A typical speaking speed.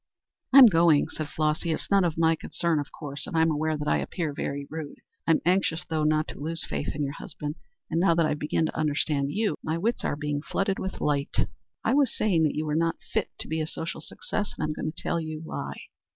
No: fast, 240 wpm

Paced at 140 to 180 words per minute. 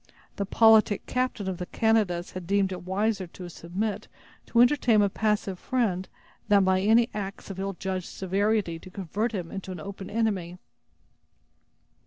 Yes: average, 160 wpm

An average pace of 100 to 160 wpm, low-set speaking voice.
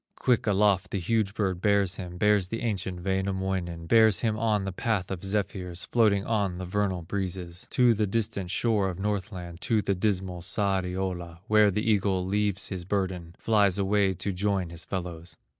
No: average, 175 wpm; very low, 95 Hz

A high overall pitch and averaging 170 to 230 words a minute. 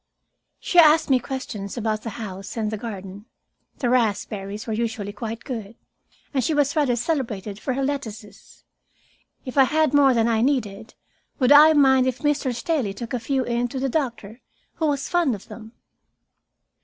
Yes: high, 240 Hz; average, 175 wpm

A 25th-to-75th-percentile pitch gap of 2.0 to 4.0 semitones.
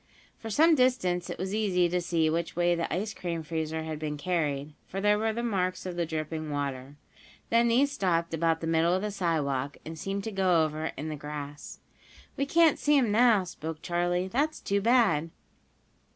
No: average, 4.7 semitones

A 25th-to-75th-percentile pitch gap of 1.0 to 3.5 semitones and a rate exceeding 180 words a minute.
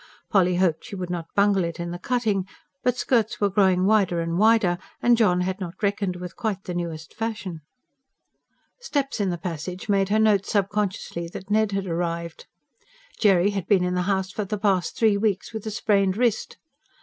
Yes: average, 2.9 semitones; average, 190 wpm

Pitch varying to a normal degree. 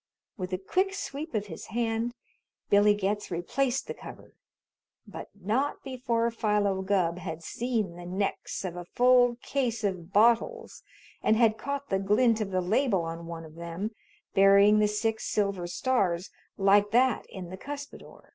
Yes: average, 4.4 semitones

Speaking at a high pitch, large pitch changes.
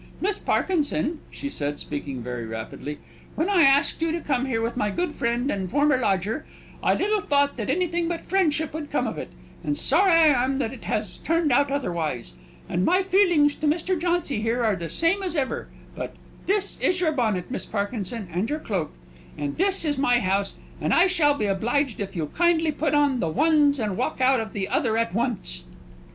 Yes: very high, 275 Hz; wide, 7.7 semitones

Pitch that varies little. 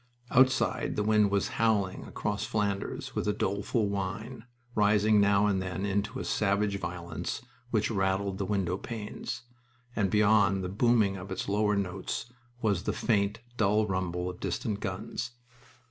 Yes: narrow, 1.8 semitones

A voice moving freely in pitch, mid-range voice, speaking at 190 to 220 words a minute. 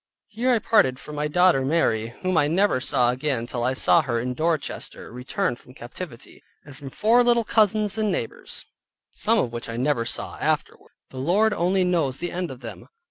Yes: wide, 6.8 semitones; medium, 150 Hz; average, 195 wpm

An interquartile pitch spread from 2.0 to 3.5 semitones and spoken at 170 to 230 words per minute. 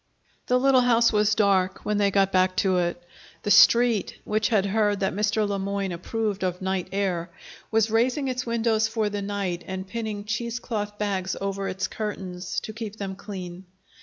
Yes: narrow, 2.6 semitones; average, 180 wpm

